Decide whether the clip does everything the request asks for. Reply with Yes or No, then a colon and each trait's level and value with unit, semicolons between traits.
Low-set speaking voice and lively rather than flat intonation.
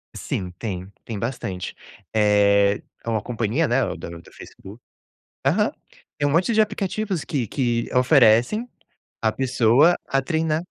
Yes: low, 120 Hz; wide, 6.7 semitones